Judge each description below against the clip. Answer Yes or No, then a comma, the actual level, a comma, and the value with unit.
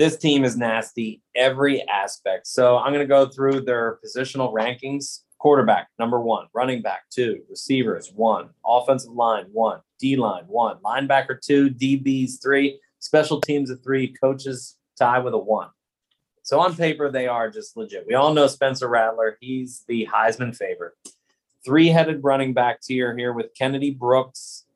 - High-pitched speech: No, low, 135 Hz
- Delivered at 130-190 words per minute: Yes, average, 160 wpm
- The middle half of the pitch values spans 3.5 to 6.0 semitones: No, narrow, 2.5 semitones